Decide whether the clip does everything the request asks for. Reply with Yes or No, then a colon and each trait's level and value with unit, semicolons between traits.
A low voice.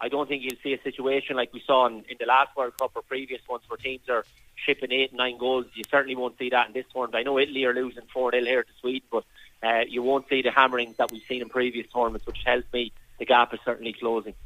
Yes: low, 125 Hz